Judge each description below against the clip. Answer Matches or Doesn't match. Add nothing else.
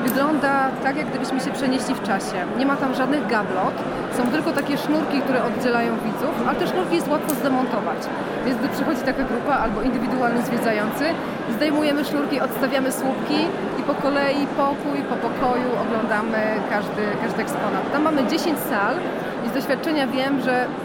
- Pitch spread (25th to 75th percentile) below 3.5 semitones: Matches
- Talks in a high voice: Matches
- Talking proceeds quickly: Matches